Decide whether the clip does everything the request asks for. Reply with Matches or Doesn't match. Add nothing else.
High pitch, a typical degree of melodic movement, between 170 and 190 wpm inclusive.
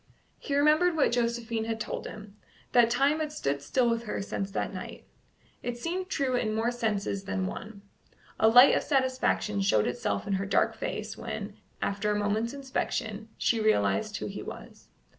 Matches